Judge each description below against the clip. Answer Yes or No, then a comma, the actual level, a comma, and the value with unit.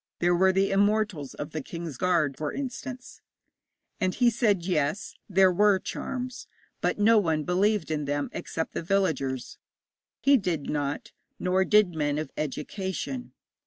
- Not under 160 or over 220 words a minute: No, average, 150 wpm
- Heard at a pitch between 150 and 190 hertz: Yes, medium, 185 Hz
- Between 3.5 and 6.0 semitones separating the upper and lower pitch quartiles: Yes, average, 5.2 semitones